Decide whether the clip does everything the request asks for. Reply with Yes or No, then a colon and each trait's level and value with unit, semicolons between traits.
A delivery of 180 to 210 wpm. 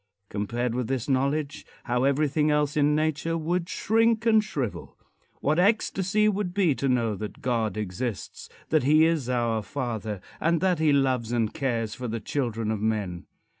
No: average, 170 wpm